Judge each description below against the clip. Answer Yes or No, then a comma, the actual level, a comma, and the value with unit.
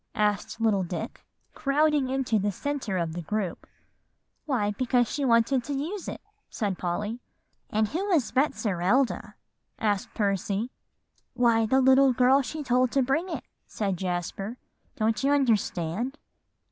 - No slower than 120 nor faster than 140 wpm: Yes, slow, 135 wpm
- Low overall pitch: No, high, 230 Hz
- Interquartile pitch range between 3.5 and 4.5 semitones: No, average, 5.0 semitones